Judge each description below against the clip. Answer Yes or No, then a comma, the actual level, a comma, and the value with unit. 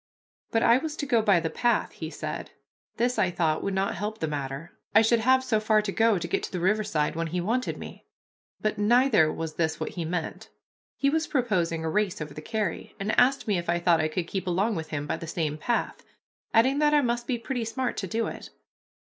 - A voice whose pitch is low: No, high, 205 Hz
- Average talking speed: No, fast, 235 wpm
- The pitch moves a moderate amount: No, wide, 6.1 semitones